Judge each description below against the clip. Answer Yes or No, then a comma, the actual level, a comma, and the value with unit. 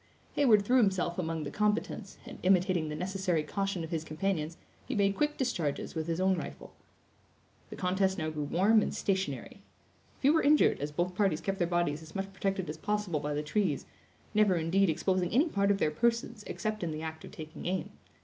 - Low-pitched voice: No, medium, 185 Hz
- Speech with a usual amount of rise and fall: Yes, average, 4.0 semitones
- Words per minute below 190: No, average, 200 wpm